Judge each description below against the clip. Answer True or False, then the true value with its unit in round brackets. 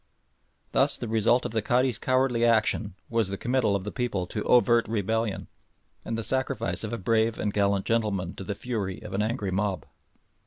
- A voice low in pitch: True (110 Hz)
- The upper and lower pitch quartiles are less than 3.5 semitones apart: True (2.8 semitones)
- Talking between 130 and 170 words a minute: False (195 wpm)